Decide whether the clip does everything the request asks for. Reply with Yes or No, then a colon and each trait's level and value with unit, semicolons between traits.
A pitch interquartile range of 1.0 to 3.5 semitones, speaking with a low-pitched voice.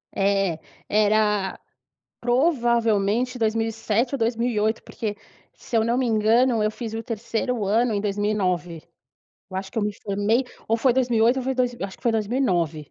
No: average, 2.8 semitones; high, 225 Hz